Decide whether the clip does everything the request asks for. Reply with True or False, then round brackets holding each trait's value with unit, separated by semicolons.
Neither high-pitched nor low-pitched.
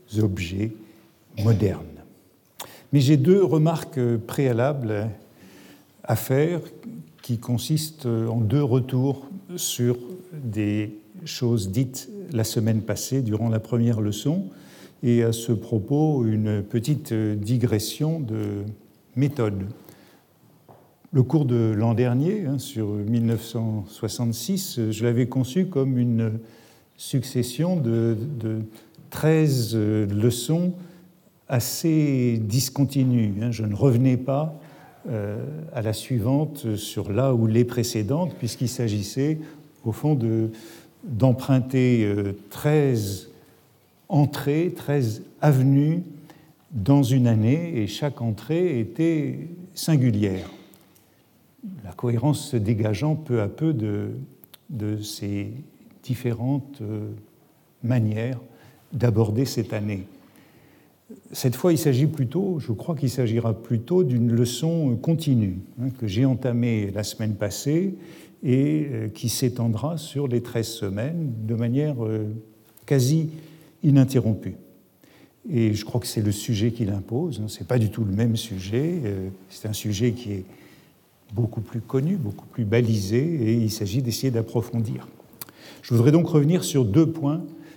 False (120 Hz)